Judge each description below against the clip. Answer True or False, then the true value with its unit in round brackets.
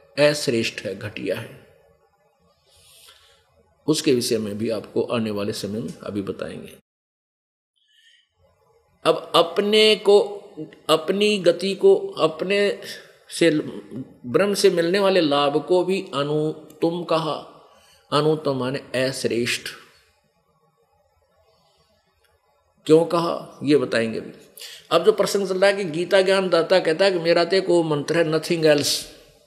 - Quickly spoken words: False (120 wpm)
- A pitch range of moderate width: True (4.9 semitones)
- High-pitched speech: False (165 Hz)